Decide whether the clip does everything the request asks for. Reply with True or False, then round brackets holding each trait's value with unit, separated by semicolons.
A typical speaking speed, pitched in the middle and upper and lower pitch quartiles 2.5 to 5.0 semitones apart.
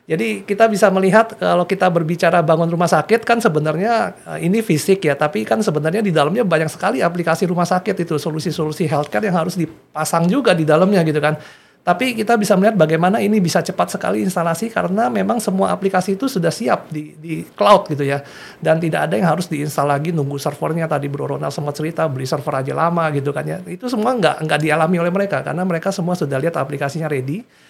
False (200 wpm; 170 Hz; 4.1 semitones)